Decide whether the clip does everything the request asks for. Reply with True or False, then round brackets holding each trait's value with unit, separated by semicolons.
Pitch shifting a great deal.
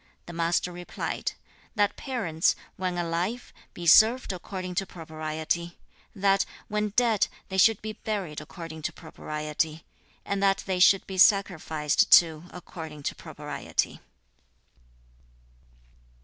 False (3.6 semitones)